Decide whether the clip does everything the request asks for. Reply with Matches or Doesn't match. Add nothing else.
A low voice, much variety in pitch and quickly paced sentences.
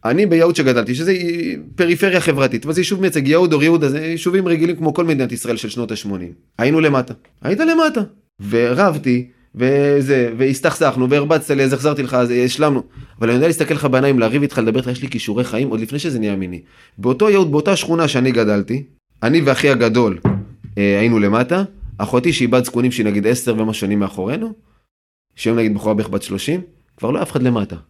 Matches